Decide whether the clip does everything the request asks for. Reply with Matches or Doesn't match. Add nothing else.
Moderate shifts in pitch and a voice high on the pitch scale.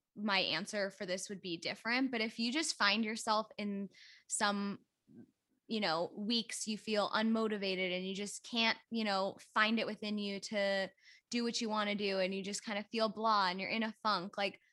Doesn't match